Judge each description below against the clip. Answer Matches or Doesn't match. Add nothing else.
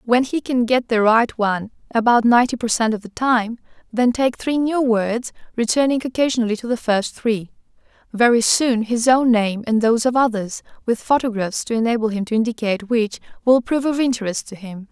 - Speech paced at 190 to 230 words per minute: Matches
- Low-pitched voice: Doesn't match